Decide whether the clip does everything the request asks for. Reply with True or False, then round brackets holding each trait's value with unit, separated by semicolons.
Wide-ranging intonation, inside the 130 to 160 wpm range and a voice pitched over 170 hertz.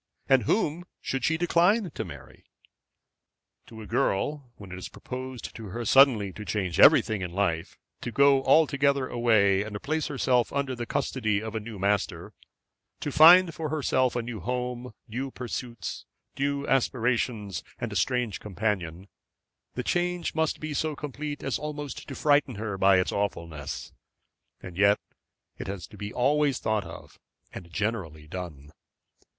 False (5.7 semitones; 155 wpm; 120 Hz)